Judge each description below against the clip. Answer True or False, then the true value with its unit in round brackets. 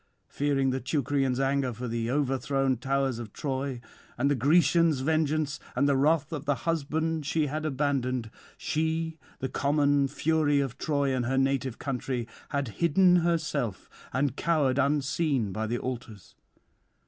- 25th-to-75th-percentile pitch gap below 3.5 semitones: True (2.8 semitones)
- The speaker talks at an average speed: True (150 wpm)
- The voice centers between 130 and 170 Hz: True (140 Hz)